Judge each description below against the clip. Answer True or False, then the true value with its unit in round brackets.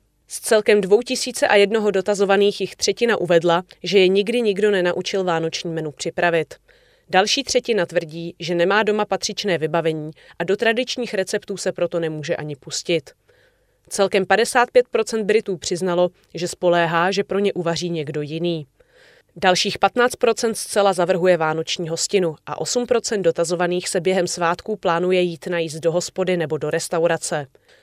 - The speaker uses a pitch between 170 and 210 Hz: True (185 Hz)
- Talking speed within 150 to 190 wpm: False (140 wpm)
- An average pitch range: True (3.9 semitones)